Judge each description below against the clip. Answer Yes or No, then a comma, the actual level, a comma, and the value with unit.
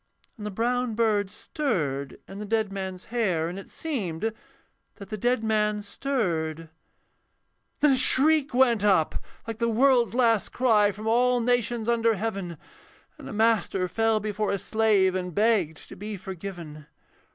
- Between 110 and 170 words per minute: Yes, average, 155 wpm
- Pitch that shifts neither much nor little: Yes, average, 3.7 semitones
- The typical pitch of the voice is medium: No, high, 215 Hz